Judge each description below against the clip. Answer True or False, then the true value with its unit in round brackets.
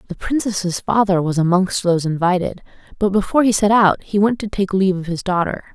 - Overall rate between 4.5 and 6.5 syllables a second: True (5.8 syllables/s)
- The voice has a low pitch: False (190 Hz)